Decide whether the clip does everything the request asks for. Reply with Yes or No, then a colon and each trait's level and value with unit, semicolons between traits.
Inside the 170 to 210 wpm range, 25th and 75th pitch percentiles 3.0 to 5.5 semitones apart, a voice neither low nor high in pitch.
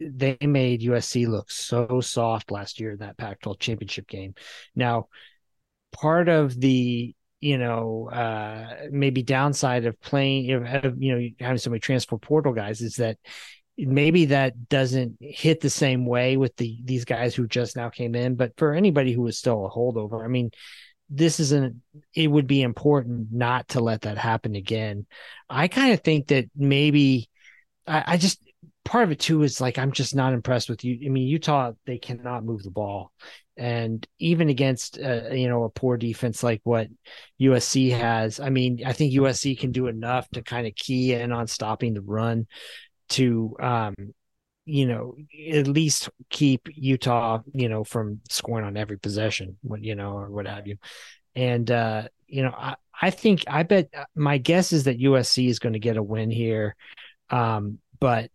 No: average, 185 wpm; average, 3.3 semitones; low, 125 Hz